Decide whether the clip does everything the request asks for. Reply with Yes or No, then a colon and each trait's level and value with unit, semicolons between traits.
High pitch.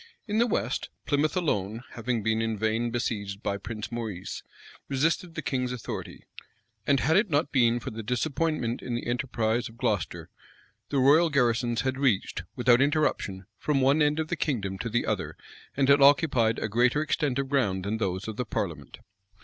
No: low, 125 Hz